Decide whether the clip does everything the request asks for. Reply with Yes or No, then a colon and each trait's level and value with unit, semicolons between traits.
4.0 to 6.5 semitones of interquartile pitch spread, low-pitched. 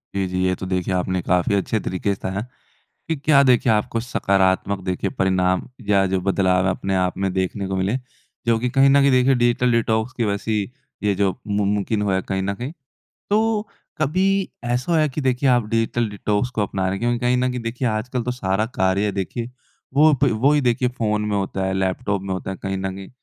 Yes: average, 4.5 semitones; low, 105 Hz